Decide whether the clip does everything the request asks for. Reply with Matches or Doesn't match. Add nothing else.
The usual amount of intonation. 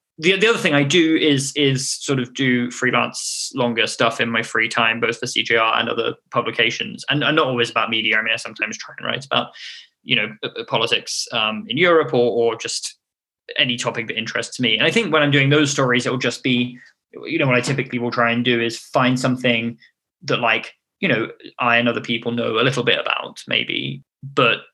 Matches